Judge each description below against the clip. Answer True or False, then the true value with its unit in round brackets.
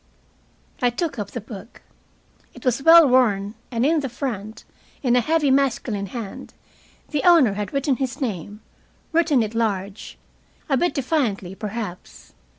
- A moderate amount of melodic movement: True (5.0 semitones)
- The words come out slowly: False (150 wpm)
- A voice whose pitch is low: False (240 Hz)